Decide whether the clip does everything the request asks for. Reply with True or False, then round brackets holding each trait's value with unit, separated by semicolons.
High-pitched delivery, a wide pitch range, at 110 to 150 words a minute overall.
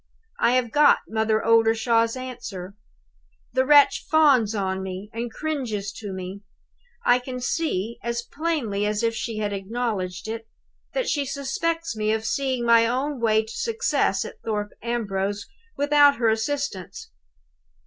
False (230 Hz; 4.1 semitones; 145 wpm)